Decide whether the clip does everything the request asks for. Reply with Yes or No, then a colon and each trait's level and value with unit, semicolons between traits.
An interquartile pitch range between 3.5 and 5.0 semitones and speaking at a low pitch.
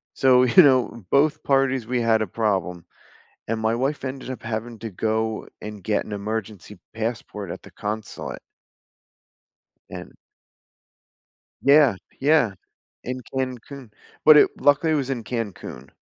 Yes: average, 3.8 semitones; low, 115 Hz